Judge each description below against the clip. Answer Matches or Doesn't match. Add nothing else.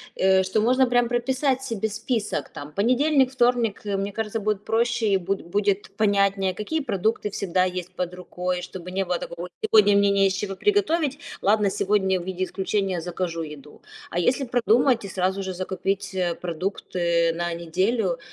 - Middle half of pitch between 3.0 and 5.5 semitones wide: Matches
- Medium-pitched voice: Doesn't match